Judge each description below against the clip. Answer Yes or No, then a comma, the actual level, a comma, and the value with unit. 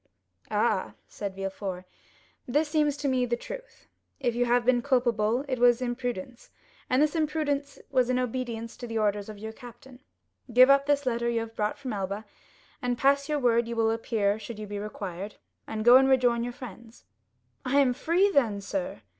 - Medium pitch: No, high, 240 Hz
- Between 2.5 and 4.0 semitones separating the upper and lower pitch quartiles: Yes, average, 3.3 semitones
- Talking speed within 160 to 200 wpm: Yes, average, 190 wpm